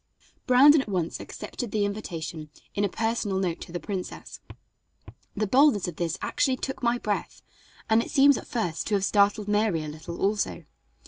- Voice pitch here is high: Yes, high, 205 Hz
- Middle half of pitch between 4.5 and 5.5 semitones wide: Yes, average, 5.0 semitones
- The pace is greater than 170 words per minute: Yes, average, 180 wpm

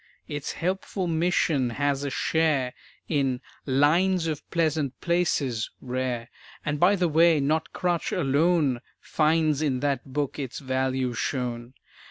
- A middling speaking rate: No, slow, 130 wpm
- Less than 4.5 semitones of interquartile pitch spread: Yes, average, 3.9 semitones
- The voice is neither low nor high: Yes, medium, 145 Hz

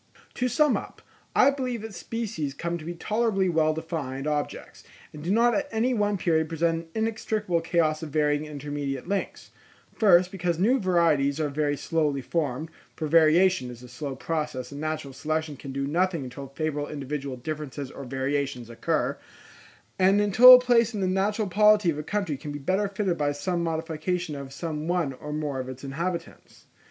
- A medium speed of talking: Yes, average, 185 wpm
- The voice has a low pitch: No, medium, 160 Hz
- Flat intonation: No, average, 4.8 semitones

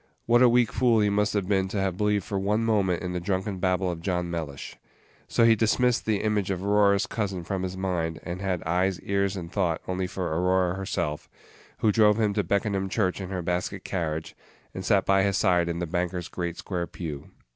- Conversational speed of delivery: No, fast, 215 wpm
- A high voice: No, very low, 95 Hz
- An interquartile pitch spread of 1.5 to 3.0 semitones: Yes, narrow, 2.4 semitones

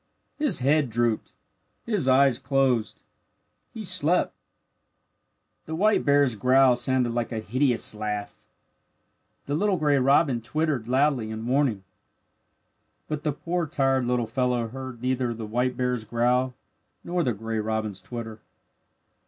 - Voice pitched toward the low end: Yes, low, 125 Hz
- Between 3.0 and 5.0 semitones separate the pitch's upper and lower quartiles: Yes, average, 3.4 semitones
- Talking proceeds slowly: Yes, slow, 130 wpm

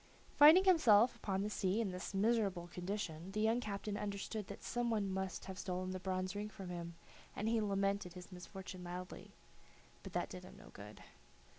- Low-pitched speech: No, high, 195 Hz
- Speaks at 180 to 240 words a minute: Yes, average, 185 wpm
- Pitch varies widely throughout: No, narrow, 2.5 semitones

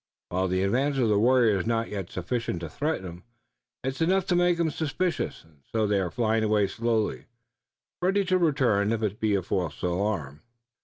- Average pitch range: No, wide, 6.5 semitones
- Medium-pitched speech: No, low, 110 Hz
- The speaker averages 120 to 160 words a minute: No, average, 195 wpm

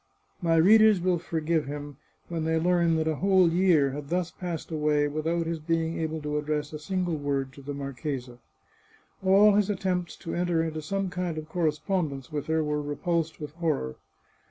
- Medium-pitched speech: Yes, medium, 160 Hz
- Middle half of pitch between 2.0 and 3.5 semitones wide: Yes, average, 2.9 semitones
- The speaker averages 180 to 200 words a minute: Yes, average, 190 wpm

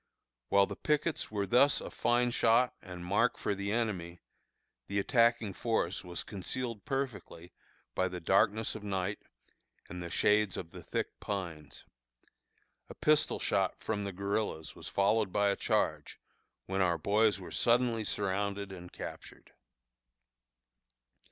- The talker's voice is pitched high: No, low, 100 Hz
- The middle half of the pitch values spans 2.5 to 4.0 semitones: Yes, average, 3.5 semitones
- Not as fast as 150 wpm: Yes, average, 140 wpm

